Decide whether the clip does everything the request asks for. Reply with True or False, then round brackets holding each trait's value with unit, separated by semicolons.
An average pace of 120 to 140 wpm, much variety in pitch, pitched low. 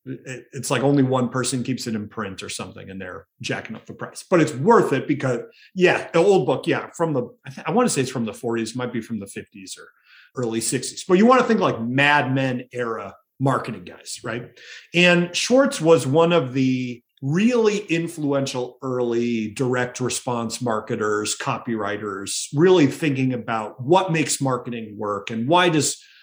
False (190 wpm; 5.8 semitones; 130 Hz)